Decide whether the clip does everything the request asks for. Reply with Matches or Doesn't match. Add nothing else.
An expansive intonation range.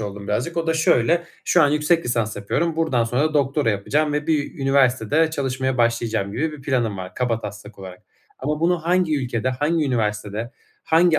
Matches